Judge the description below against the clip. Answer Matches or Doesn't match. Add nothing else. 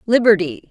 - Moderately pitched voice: Doesn't match